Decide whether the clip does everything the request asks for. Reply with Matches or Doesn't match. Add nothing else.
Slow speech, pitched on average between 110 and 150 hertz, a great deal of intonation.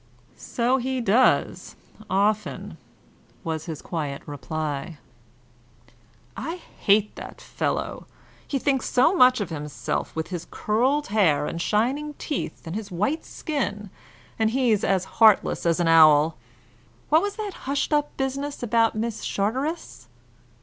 Doesn't match